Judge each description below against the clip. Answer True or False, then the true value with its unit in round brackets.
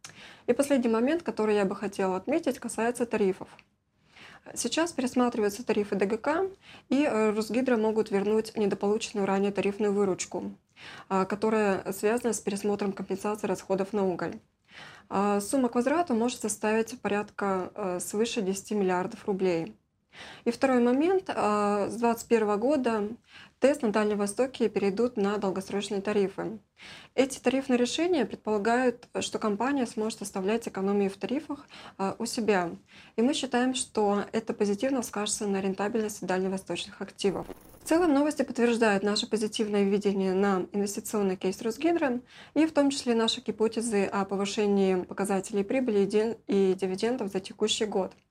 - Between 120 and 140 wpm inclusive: True (130 wpm)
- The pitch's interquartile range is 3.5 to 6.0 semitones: False (3.1 semitones)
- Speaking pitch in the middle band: False (215 Hz)